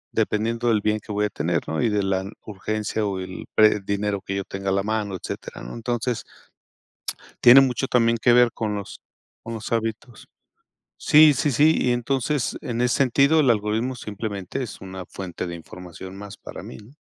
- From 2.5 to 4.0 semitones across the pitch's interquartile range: Yes, average, 3.7 semitones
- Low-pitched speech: Yes, low, 110 Hz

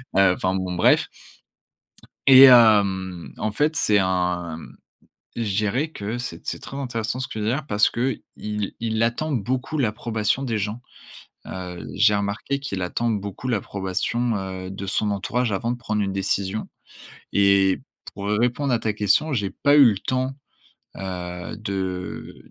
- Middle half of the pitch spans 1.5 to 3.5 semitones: No, average, 4.1 semitones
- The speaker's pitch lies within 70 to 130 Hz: Yes, low, 105 Hz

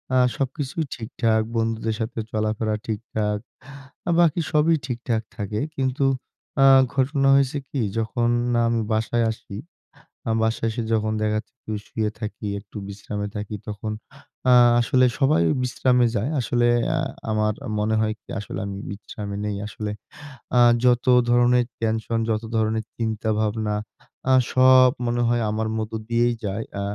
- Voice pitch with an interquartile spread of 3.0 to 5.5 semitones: No, narrow, 2.4 semitones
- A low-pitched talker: Yes, low, 115 Hz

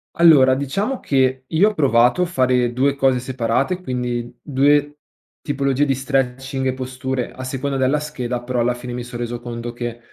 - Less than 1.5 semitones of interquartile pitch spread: No, narrow, 2.4 semitones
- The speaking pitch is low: Yes, low, 130 Hz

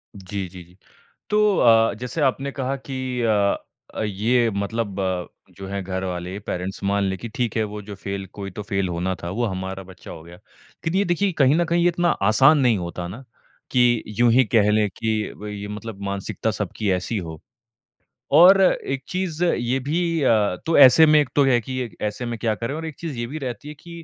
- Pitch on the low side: Yes, low, 110 Hz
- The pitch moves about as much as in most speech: No, wide, 5.8 semitones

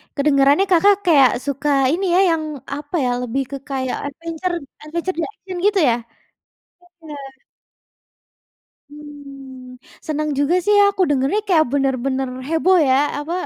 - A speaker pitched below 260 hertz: No, very high, 295 Hz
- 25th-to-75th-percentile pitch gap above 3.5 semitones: Yes, average, 3.9 semitones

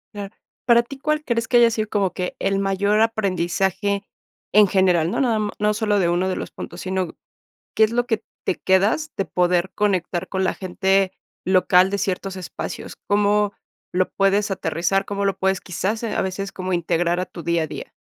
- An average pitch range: No, narrow, 2.2 semitones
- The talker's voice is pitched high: Yes, high, 195 Hz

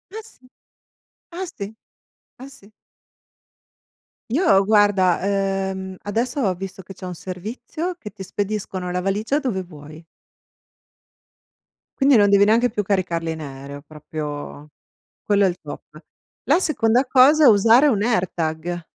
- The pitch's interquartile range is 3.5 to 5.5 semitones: Yes, average, 4.3 semitones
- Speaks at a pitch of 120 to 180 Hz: No, high, 195 Hz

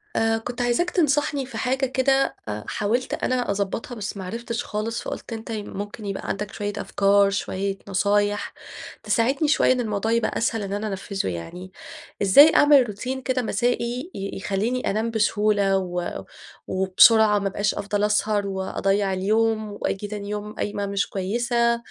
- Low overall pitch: No, high, 210 Hz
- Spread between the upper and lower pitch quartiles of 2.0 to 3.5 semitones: Yes, average, 3.2 semitones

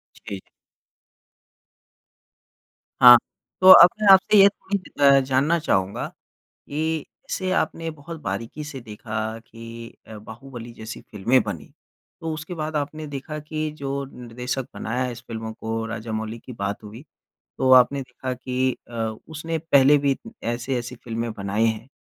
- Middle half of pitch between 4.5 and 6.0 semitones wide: Yes, average, 5.0 semitones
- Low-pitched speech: Yes, low, 130 Hz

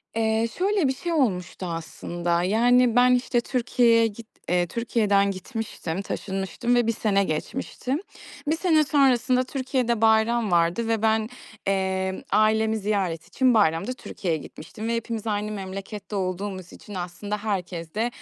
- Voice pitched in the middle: No, high, 215 Hz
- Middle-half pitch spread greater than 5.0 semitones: No, average, 4.0 semitones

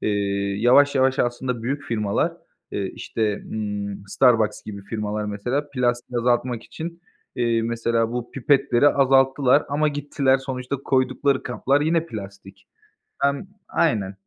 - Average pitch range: Yes, average, 3.8 semitones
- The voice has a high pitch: No, low, 125 Hz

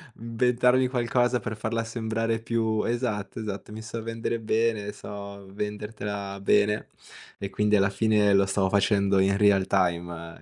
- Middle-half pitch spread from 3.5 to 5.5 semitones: No, narrow, 2.4 semitones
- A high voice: No, low, 105 Hz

